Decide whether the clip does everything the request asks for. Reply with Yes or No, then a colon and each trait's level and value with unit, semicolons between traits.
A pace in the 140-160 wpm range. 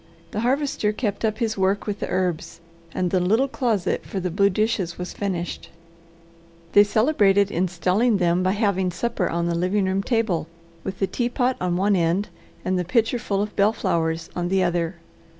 No: average, 180 wpm